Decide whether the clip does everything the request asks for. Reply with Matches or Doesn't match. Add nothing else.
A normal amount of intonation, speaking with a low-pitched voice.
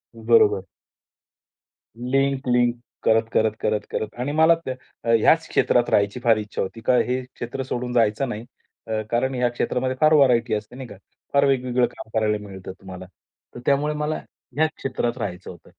Matches